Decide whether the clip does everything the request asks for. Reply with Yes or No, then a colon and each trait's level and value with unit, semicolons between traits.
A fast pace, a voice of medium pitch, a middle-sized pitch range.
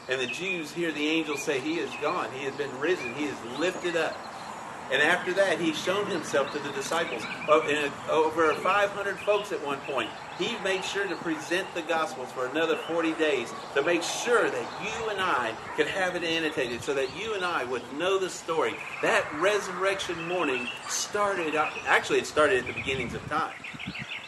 No: average, 190 wpm; medium, 180 Hz; average, 3.8 semitones